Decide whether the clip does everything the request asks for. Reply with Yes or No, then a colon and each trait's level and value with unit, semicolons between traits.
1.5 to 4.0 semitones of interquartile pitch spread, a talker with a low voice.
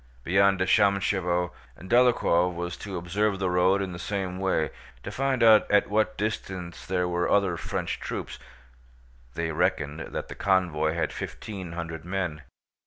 Yes: narrow, 2.4 semitones; very low, 90 Hz